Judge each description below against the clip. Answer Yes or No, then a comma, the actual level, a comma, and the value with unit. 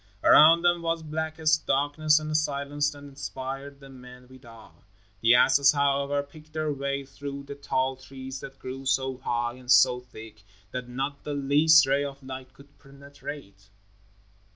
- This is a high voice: No, medium, 140 Hz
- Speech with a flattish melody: Yes, narrow, 1.9 semitones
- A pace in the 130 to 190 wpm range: Yes, average, 165 wpm